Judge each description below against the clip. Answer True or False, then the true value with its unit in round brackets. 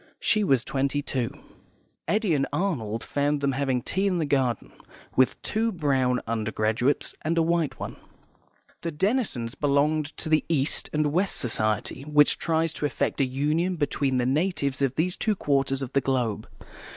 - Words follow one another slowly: False (165 wpm)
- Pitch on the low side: False (145 Hz)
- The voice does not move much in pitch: False (3.9 semitones)